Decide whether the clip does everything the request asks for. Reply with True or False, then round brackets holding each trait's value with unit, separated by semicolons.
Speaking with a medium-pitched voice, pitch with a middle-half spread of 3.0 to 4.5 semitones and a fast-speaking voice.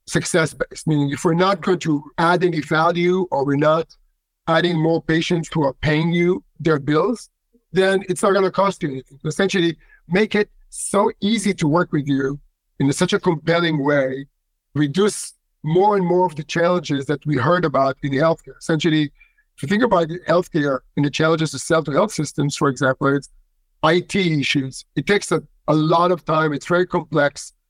False (160 Hz; 3.6 semitones; 190 wpm)